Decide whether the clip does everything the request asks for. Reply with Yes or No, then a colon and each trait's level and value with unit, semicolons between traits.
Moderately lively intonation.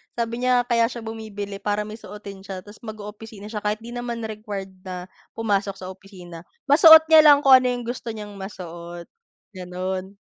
Yes: average, 3.3 semitones